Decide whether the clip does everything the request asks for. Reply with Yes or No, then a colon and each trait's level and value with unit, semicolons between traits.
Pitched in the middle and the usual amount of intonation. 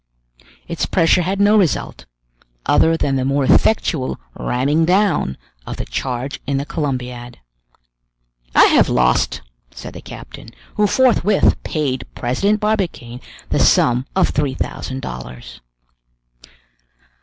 No: medium, 145 Hz; wide, 6.9 semitones